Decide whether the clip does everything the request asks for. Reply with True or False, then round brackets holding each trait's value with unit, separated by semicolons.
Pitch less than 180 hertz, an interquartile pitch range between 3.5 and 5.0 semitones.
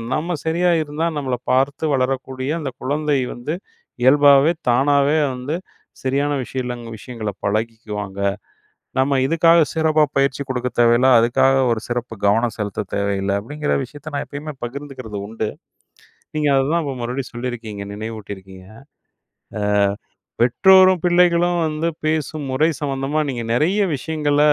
True (135 Hz; 4.2 semitones)